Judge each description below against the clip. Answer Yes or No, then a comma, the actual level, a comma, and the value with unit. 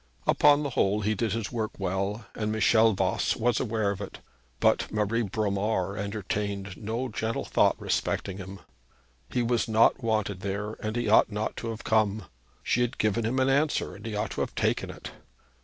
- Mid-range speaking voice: No, low, 110 Hz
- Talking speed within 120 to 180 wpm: No, average, 190 wpm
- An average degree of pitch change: No, narrow, 2.3 semitones